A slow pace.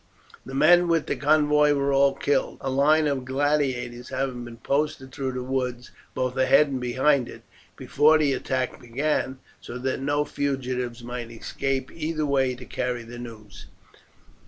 No: average, 160 wpm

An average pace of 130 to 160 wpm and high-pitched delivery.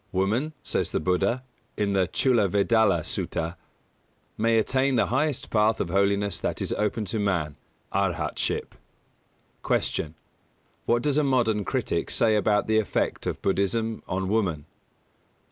No: average, 140 wpm; low, 105 Hz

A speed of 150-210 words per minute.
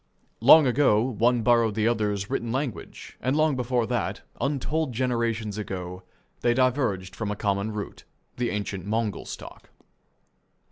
No: average, 140 wpm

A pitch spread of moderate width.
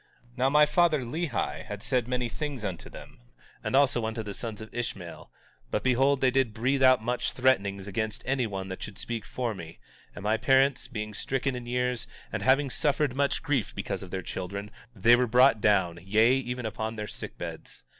Yes: average, 3.8 semitones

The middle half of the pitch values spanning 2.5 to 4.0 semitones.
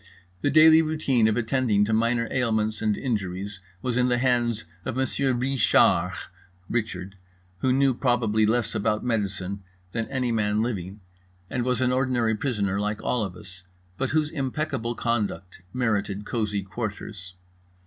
Yes: average, 3.5 semitones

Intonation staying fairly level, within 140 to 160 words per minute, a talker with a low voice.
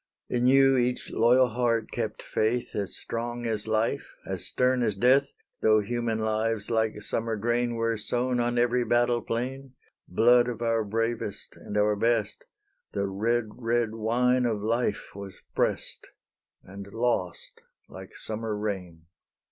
Yes: narrow, 2.2 semitones; average, 145 wpm; low, 115 Hz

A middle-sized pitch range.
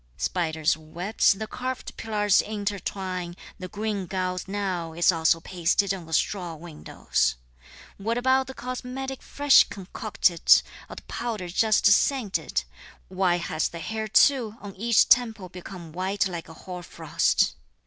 Yes: average, 4.1 semitones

